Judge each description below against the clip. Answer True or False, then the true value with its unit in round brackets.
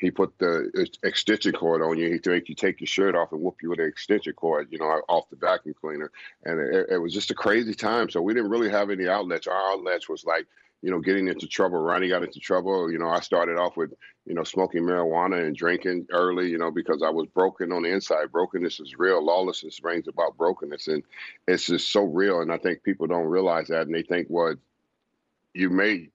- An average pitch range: False (9.0 semitones)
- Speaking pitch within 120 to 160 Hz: False (90 Hz)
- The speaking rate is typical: False (230 wpm)